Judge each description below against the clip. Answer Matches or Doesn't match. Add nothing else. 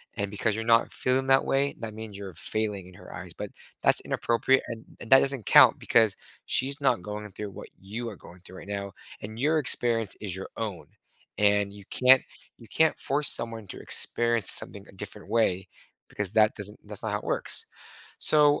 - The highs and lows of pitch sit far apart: Doesn't match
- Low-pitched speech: Matches